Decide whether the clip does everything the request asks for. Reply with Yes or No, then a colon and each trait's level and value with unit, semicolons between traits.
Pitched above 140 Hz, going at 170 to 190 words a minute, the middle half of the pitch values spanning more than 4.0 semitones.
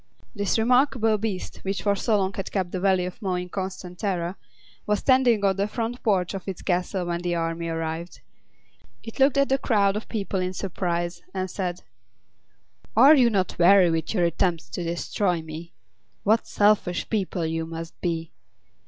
No: high, 190 Hz; average, 180 wpm; average, 3.3 semitones